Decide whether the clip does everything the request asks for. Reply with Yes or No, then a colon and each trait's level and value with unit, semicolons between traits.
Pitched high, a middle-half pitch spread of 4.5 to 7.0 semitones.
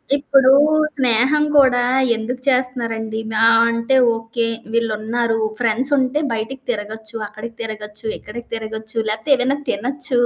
No: high, 230 Hz; average, 2.7 semitones